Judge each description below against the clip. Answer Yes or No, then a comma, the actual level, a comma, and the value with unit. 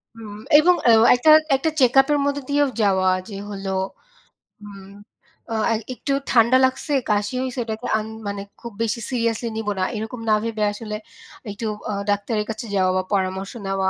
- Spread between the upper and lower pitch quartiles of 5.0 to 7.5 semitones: No, average, 3.4 semitones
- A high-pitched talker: Yes, high, 220 Hz